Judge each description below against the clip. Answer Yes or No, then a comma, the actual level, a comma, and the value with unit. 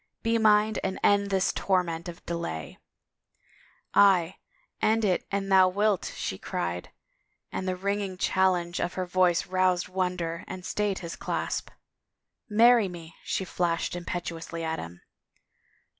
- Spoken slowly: No, average, 150 wpm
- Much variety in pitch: No, narrow, 2.6 semitones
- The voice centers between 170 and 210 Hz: Yes, medium, 185 Hz